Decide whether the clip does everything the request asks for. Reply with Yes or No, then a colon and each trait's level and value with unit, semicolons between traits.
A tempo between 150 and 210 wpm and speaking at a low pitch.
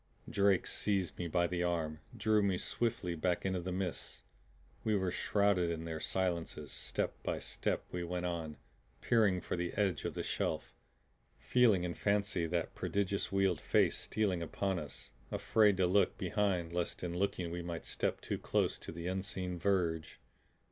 Yes: average, 170 wpm; very low, 90 Hz